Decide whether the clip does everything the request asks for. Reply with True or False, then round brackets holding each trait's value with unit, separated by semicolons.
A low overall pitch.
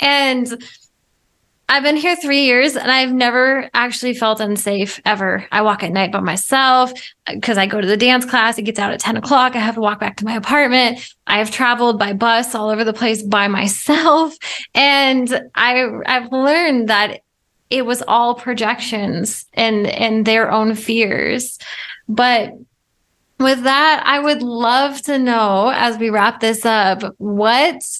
False (235 Hz)